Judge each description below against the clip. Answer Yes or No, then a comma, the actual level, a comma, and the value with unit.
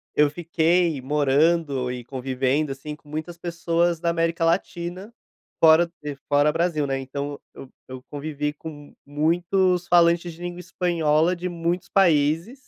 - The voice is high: No, medium, 160 Hz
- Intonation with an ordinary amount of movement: Yes, average, 3.0 semitones